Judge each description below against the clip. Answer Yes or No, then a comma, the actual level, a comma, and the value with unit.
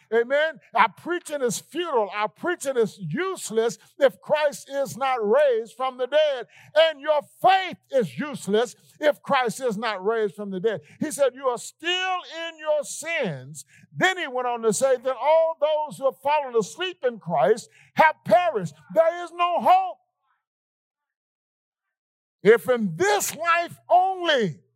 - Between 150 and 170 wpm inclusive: Yes, average, 155 wpm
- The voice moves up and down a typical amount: No, wide, 6.7 semitones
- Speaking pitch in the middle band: No, very high, 275 Hz